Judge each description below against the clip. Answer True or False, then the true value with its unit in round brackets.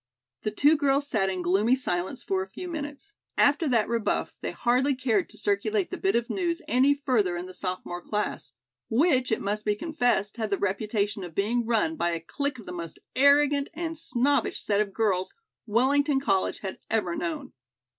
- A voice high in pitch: True (235 Hz)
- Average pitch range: False (6.3 semitones)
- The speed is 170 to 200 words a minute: True (190 wpm)